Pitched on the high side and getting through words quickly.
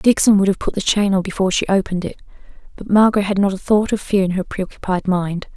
Yes: high, 195 Hz; fast, 260 wpm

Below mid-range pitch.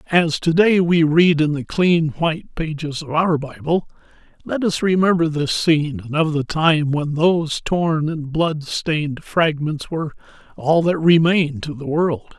No: medium, 160 Hz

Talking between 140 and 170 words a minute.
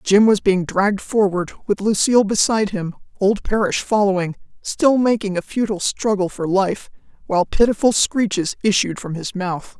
Yes: average, 160 wpm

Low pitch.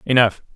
Yes: low, 115 Hz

